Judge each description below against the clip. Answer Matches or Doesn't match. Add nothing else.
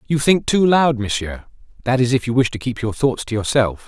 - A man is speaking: Matches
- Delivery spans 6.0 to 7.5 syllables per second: Doesn't match